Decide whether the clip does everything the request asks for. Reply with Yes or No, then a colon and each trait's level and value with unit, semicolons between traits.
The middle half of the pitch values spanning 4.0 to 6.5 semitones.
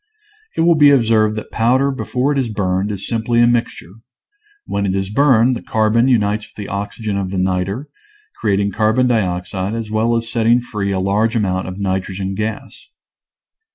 No: average, 3.2 semitones